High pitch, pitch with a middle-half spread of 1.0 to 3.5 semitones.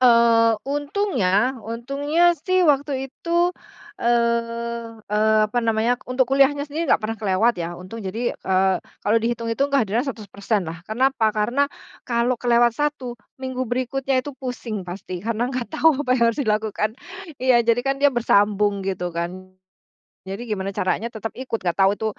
No: high, 235 Hz; average, 4.0 semitones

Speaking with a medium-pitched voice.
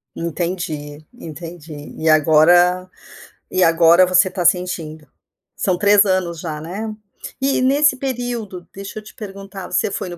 Yes: medium, 180 Hz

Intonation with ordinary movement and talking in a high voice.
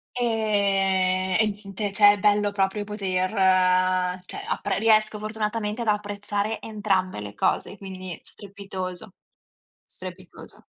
No: narrow, 2.1 semitones; high, 200 Hz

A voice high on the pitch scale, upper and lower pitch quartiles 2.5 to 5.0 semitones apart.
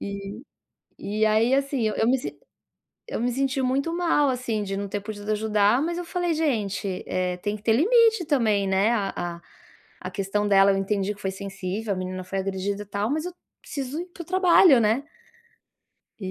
No: high, 215 Hz; wide, 5.6 semitones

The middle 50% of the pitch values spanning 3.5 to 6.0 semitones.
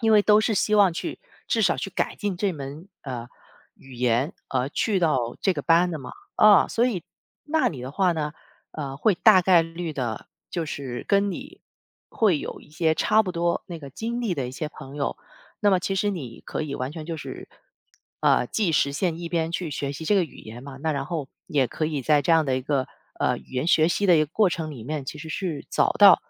Yes: average, 5.2 semitones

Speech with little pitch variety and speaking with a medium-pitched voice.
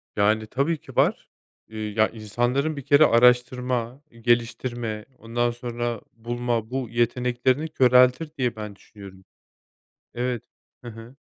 No: narrow, 1.9 semitones; low, 120 Hz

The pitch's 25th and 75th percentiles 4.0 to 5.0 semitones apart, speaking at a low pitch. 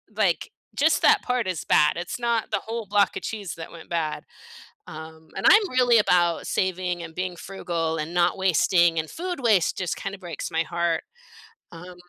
No: average, 4.4 semitones; medium, 180 Hz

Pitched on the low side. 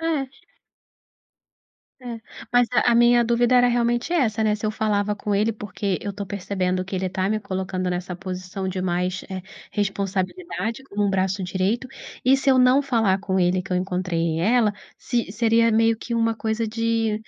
No: high, 210 Hz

